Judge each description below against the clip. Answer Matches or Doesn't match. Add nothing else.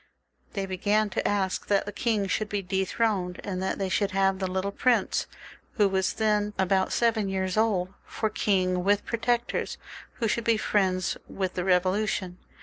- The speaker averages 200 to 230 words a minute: Doesn't match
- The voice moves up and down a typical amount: Doesn't match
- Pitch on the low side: Doesn't match